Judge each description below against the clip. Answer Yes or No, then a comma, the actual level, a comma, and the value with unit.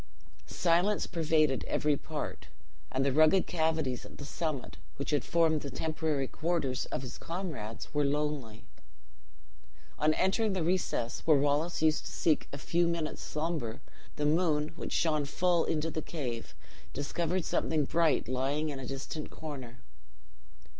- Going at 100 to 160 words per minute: Yes, average, 145 wpm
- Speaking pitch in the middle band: Yes, medium, 155 Hz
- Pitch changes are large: No, average, 3.0 semitones